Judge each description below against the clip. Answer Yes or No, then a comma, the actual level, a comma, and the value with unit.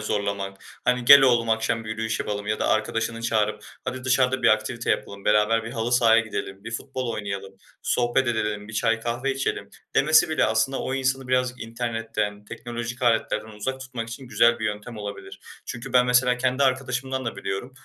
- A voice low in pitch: Yes, low, 115 Hz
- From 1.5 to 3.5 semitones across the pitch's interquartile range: Yes, average, 2.9 semitones